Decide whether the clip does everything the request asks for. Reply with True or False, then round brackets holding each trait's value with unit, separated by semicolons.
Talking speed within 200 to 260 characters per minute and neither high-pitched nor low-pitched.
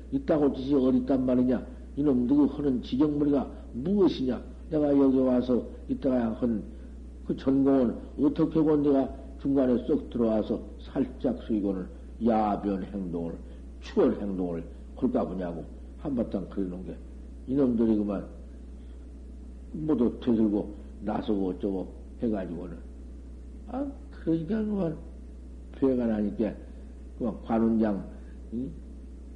False (250 characters per minute; 100 Hz)